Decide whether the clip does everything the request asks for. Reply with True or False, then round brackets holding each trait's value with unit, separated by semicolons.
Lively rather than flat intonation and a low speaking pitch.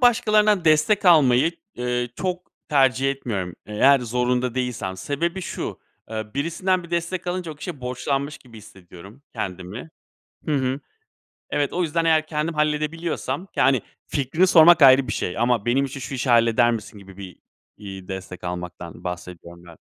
True (6.8 semitones; 130 Hz)